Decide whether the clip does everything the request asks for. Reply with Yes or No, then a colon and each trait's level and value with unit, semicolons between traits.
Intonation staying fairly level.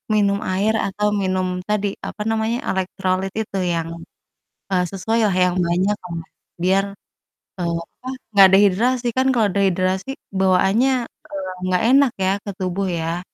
Yes: narrow, 2.2 semitones